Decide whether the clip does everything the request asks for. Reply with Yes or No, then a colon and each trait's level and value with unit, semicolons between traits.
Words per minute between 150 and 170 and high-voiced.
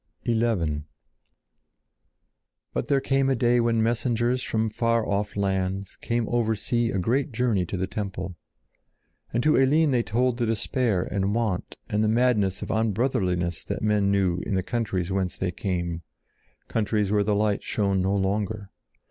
No: average, 160 wpm; low, 105 Hz